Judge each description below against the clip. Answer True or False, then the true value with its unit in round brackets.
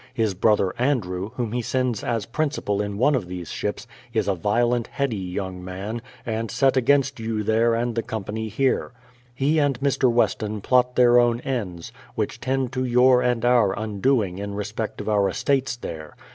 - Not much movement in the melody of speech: False (3.5 semitones)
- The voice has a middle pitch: False (115 Hz)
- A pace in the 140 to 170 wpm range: False (180 wpm)